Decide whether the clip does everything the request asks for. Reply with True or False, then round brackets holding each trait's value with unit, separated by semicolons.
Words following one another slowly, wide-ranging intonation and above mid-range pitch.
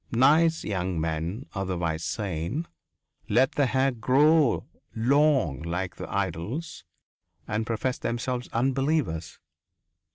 False (100 wpm; 7.7 semitones; 115 Hz)